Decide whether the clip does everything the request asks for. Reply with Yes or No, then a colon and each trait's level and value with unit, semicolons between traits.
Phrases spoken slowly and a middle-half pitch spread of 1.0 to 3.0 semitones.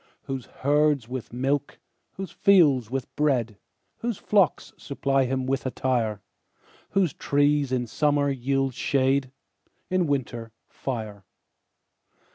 Yes: slow, 110 wpm; narrow, 2.5 semitones